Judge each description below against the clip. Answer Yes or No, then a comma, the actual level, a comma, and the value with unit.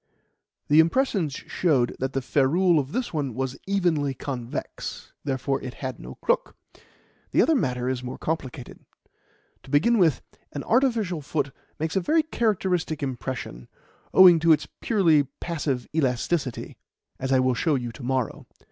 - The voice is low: No, medium, 145 Hz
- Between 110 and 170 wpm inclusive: Yes, average, 150 wpm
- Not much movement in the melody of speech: No, average, 5.0 semitones